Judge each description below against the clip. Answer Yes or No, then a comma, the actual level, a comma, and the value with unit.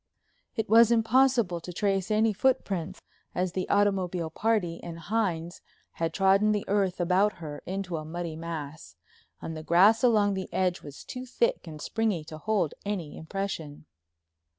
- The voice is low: No, medium, 185 Hz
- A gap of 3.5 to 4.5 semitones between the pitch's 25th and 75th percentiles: Yes, average, 4.2 semitones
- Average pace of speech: Yes, average, 155 wpm